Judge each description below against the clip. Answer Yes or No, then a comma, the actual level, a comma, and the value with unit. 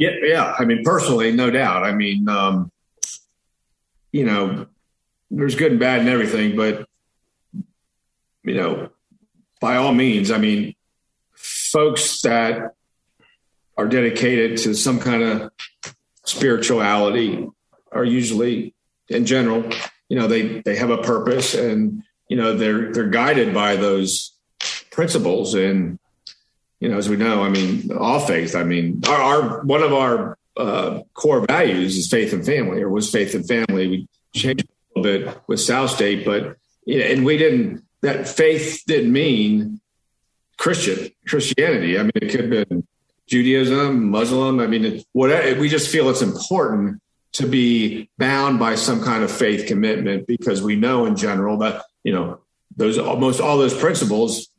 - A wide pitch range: Yes, wide, 6.1 semitones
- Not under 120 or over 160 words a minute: Yes, average, 155 wpm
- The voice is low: Yes, low, 120 Hz